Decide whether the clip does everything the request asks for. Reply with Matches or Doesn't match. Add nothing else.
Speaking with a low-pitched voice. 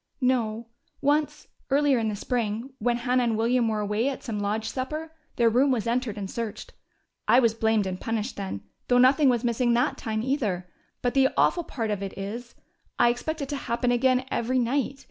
Doesn't match